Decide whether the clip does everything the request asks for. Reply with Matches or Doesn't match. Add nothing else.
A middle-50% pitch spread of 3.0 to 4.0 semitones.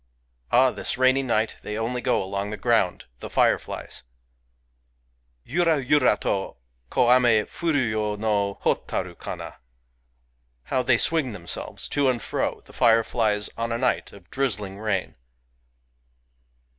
Matches